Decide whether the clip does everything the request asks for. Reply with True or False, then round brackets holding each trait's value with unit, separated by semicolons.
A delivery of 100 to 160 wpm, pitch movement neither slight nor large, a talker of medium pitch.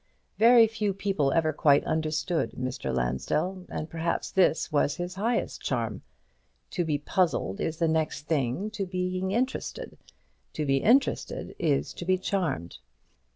True (145 wpm; 4.6 semitones; 165 Hz)